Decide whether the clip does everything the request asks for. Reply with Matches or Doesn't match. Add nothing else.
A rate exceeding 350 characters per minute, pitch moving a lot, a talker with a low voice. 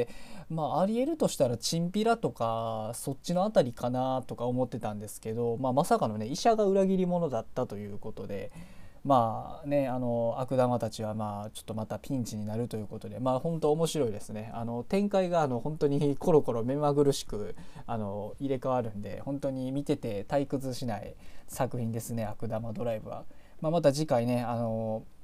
Doesn't match